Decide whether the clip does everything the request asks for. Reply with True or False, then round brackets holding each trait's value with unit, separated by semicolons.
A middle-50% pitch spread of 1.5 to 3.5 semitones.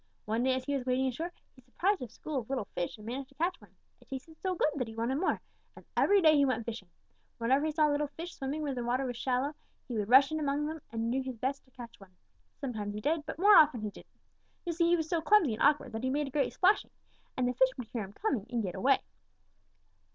False (4.4 semitones)